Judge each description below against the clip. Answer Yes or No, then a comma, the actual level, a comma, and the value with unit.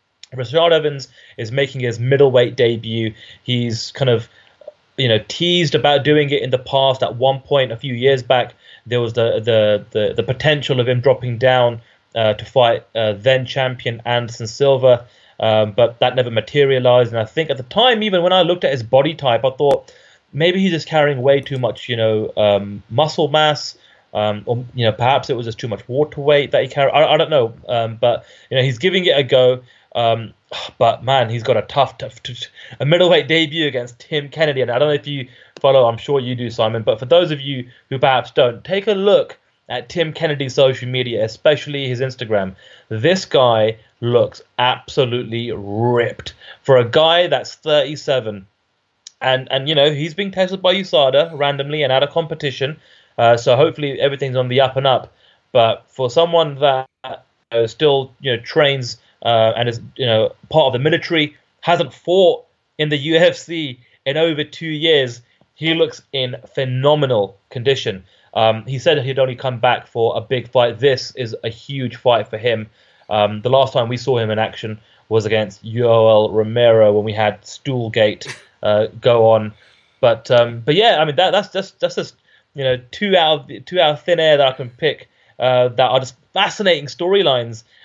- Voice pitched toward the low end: Yes, low, 130 Hz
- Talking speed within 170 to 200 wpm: Yes, average, 195 wpm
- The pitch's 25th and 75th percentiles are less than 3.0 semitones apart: No, average, 4.3 semitones